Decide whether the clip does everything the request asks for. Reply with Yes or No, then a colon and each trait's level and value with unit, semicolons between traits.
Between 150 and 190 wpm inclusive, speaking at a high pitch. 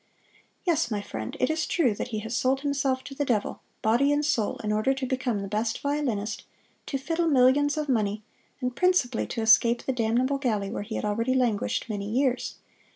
No: average, 200 wpm; very high, 250 Hz